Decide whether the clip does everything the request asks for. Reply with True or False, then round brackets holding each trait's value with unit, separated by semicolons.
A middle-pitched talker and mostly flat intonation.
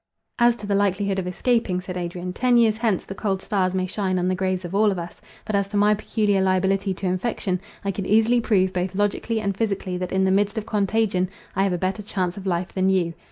False (195 Hz; 2.2 semitones)